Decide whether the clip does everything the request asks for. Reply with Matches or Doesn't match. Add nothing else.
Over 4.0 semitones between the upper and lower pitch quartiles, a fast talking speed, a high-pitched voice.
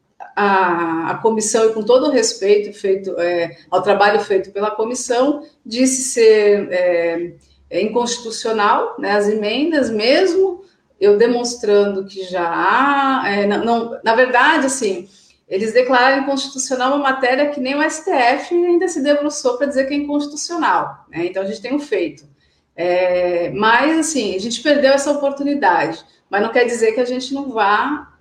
Doesn't match